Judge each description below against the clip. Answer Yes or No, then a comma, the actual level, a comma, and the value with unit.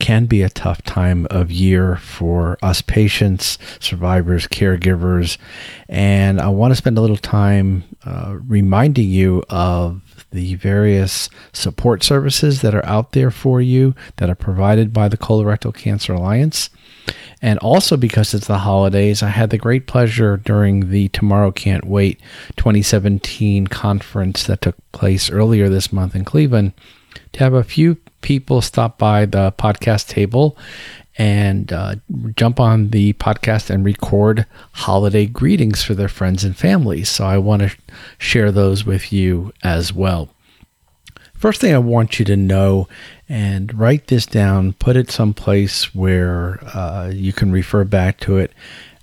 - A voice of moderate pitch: No, low, 100 Hz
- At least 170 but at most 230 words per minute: No, average, 155 wpm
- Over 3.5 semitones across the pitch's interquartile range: No, average, 2.9 semitones